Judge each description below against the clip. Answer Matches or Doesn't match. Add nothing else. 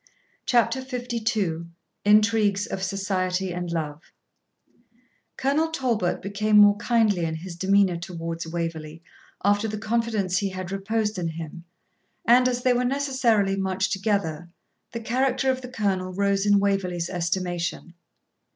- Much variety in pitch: Doesn't match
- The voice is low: Doesn't match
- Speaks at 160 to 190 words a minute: Doesn't match